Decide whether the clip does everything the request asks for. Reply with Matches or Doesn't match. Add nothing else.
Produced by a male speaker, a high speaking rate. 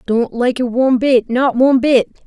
Doesn't match